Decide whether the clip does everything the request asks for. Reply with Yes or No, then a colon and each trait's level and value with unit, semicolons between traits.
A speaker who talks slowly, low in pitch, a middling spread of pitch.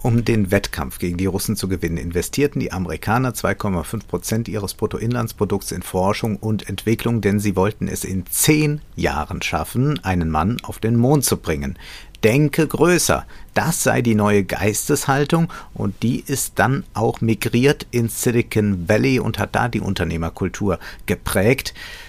No: average, 150 wpm; low, 110 Hz; average, 4.2 semitones